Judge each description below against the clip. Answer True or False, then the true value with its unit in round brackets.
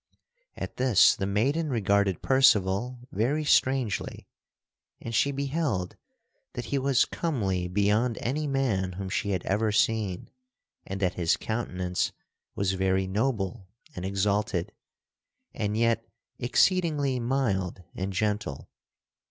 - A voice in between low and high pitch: False (105 Hz)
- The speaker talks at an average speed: False (120 wpm)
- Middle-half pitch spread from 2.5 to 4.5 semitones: False (5.3 semitones)